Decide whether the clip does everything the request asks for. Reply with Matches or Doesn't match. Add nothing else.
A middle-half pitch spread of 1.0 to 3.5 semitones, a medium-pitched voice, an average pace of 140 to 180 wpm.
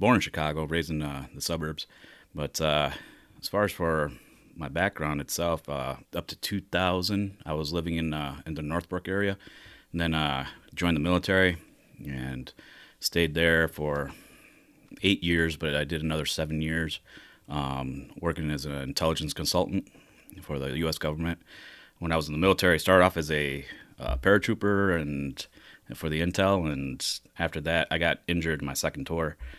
Doesn't match